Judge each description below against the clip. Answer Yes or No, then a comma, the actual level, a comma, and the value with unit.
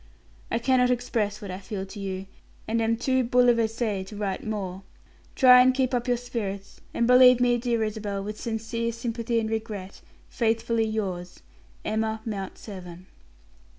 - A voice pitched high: Yes, high, 225 Hz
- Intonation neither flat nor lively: Yes, average, 3.0 semitones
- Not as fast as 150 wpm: No, average, 155 wpm